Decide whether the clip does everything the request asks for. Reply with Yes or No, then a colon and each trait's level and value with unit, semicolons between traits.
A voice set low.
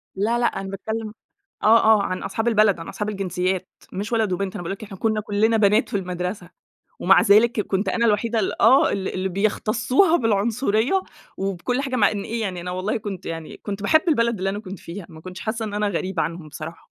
No: high, 205 Hz